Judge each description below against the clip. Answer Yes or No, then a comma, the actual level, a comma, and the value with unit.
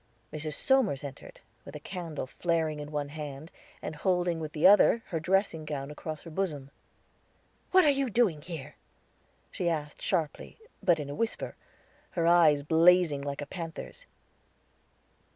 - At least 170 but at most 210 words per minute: No, average, 150 wpm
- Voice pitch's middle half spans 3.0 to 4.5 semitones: Yes, average, 3.4 semitones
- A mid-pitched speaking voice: Yes, medium, 160 Hz